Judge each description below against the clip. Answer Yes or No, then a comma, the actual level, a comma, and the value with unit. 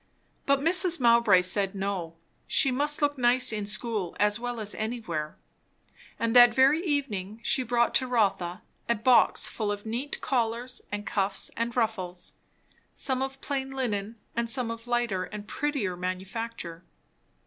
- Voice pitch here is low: No, high, 230 Hz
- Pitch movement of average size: Yes, average, 4.0 semitones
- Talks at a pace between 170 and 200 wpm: No, average, 150 wpm